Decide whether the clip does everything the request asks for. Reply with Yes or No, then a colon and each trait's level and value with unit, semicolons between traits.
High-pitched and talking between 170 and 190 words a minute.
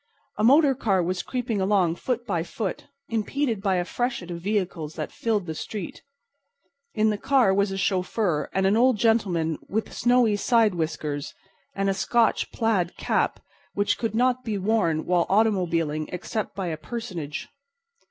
No: high, 200 Hz; average, 160 wpm